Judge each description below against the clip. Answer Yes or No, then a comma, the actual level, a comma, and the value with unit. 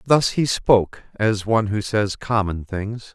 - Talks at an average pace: Yes, average, 170 wpm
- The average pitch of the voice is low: Yes, low, 105 Hz